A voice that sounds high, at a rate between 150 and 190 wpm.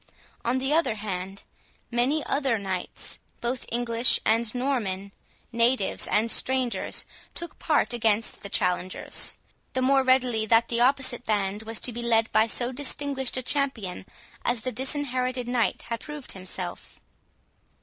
No: high, 240 Hz; average, 140 wpm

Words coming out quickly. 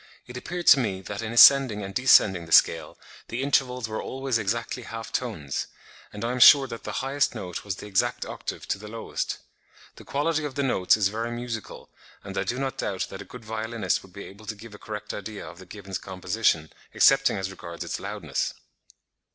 Yes: fast, 210 wpm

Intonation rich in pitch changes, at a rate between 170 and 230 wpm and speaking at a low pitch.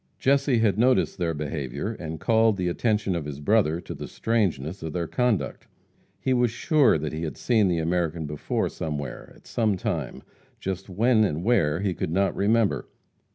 Yes: wide, 5.9 semitones; average, 180 wpm; very low, 95 Hz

